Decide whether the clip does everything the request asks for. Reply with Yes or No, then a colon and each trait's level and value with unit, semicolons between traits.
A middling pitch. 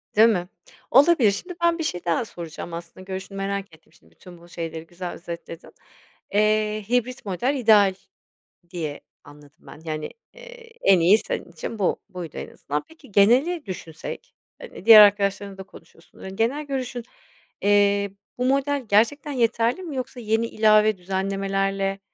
No: high, 205 Hz